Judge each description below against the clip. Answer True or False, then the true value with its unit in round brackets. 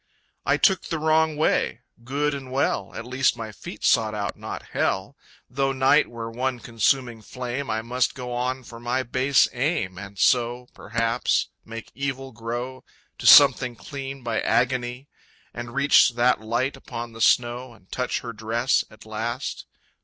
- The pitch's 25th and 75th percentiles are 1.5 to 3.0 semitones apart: True (2.5 semitones)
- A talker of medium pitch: False (125 Hz)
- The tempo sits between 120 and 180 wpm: True (160 wpm)